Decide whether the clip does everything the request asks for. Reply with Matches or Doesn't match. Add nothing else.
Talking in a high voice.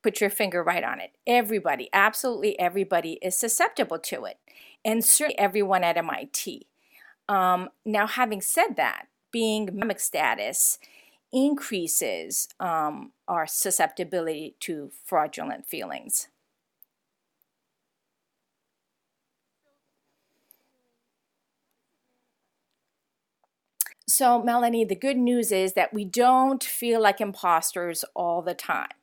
Matches